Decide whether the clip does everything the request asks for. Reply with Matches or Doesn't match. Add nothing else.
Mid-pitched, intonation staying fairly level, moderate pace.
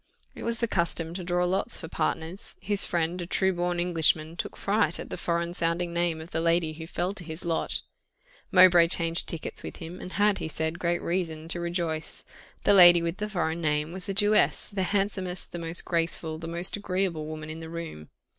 Doesn't match